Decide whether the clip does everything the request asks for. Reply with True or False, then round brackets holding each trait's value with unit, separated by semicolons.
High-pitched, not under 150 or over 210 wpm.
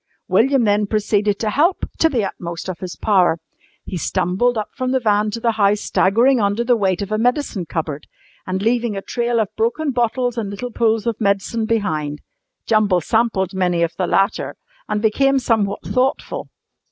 True (215 Hz; 180 wpm)